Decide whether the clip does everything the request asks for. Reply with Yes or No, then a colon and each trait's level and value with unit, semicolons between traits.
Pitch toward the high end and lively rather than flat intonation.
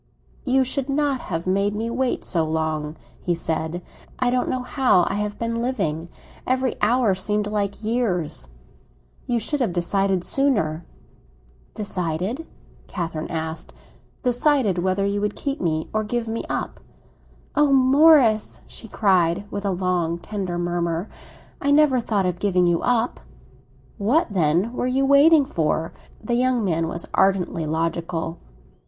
Yes: high, 200 Hz; wide, 6.4 semitones